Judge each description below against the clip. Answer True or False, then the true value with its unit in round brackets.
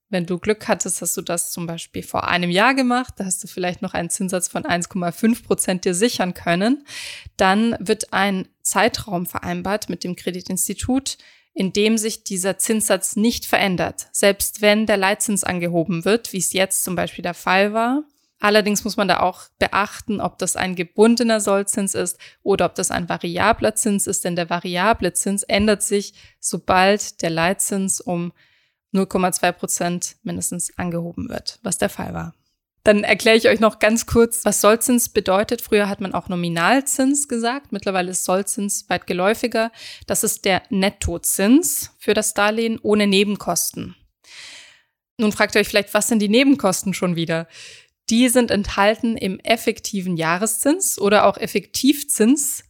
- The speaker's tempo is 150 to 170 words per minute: True (165 wpm)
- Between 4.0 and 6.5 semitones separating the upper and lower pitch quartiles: False (3.5 semitones)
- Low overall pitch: False (200 Hz)